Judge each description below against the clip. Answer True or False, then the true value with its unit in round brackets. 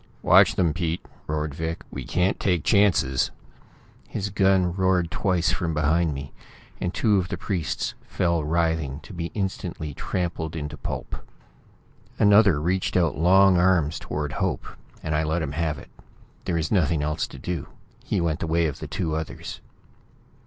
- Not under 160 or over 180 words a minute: True (165 wpm)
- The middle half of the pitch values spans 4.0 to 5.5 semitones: False (3.1 semitones)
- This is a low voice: True (85 Hz)